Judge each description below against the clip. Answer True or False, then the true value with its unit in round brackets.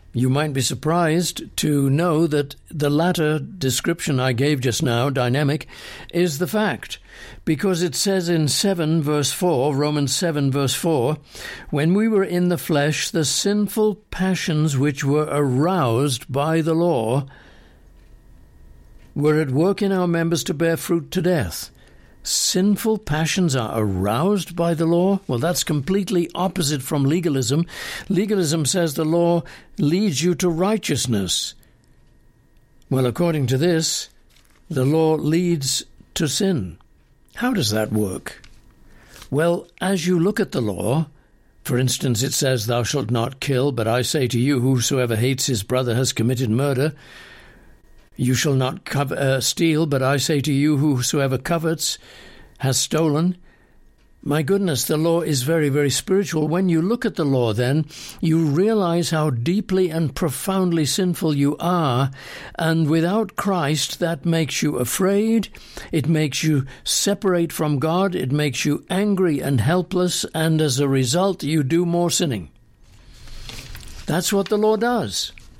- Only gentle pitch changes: False (4.7 semitones)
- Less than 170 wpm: True (150 wpm)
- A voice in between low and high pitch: True (155 Hz)